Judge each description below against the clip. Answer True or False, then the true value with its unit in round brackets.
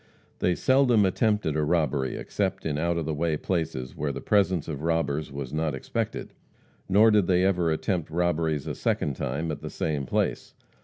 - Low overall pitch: True (80 Hz)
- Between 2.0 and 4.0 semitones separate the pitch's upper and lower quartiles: True (3.5 semitones)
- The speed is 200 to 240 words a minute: False (185 wpm)